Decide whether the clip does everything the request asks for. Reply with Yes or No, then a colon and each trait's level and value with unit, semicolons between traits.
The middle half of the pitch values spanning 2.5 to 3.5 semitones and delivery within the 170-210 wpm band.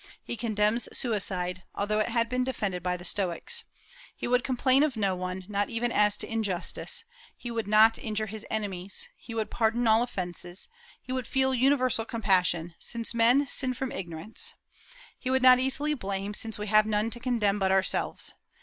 No: average, 4.0 semitones; average, 180 wpm